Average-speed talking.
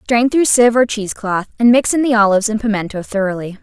No: fast, 215 wpm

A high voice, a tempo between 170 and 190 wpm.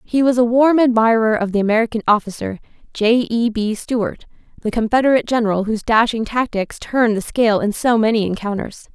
Yes: high, 225 Hz; average, 175 wpm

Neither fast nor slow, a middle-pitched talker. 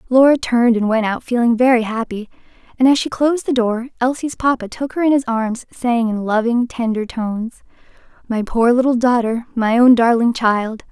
No: average, 185 wpm; high, 240 Hz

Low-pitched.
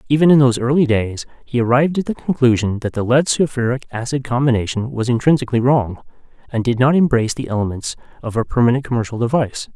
Yes: low, 125 Hz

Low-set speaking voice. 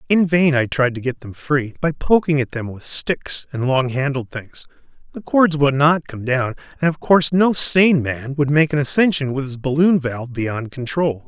No: medium, 145 Hz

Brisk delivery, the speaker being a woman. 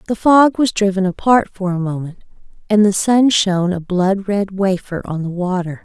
No: average, 195 wpm; female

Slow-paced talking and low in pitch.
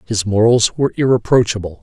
Yes: slow, 130 wpm; low, 110 Hz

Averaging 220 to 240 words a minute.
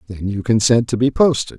Yes: fast, 225 wpm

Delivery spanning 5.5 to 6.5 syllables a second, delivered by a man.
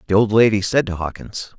Yes: 6.0 syllables/s; male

